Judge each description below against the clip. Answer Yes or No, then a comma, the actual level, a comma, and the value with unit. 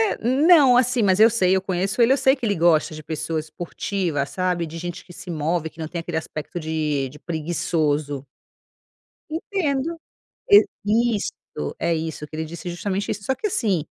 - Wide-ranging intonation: Yes, wide, 6.4 semitones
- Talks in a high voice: No, medium, 175 Hz